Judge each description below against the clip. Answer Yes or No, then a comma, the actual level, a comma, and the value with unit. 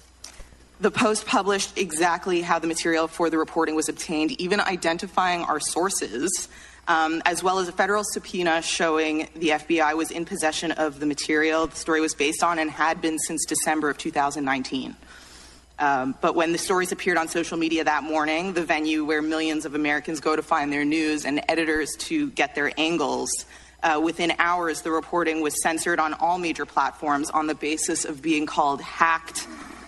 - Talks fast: No, average, 180 wpm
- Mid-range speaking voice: Yes, medium, 160 Hz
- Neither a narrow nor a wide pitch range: No, narrow, 1.8 semitones